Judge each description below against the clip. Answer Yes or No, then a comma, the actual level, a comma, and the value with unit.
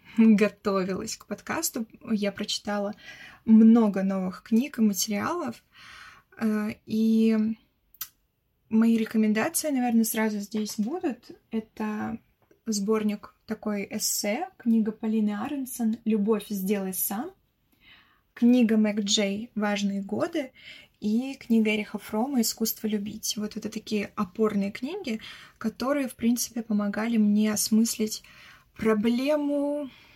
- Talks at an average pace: No, slow, 100 wpm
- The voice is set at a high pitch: Yes, high, 220 Hz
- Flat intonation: Yes, narrow, 1.9 semitones